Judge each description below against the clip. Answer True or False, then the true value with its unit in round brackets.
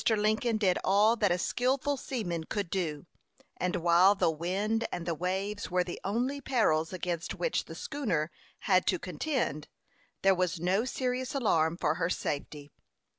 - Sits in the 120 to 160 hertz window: False (185 Hz)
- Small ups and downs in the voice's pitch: False (4.8 semitones)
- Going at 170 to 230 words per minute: False (160 wpm)